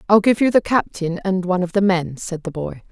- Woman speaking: Yes, female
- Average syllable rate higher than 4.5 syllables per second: Yes, 5.6 syllables/s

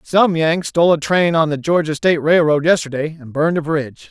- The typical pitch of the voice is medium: Yes, medium, 160 Hz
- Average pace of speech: No, fast, 220 wpm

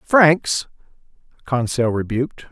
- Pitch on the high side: No, medium, 140 Hz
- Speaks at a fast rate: No, slow, 70 wpm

